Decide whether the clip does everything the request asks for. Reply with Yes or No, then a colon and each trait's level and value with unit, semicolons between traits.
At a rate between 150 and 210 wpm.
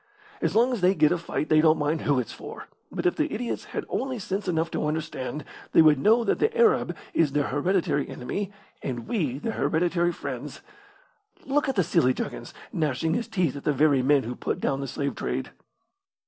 Yes: fast, 205 wpm